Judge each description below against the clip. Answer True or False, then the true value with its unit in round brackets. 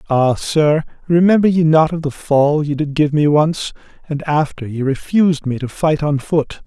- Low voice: False (150 Hz)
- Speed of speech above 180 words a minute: True (200 wpm)